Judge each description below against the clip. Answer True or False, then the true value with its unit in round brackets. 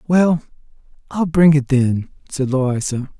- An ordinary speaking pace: False (130 wpm)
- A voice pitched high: False (145 Hz)